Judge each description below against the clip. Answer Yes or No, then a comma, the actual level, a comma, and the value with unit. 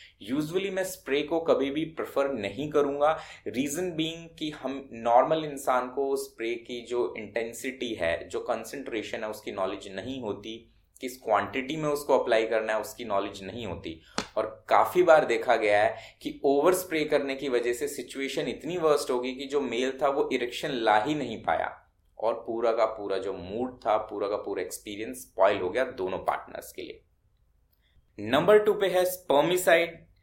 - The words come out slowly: No, average, 175 wpm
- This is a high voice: No, medium, 140 Hz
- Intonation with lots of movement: Yes, wide, 5.7 semitones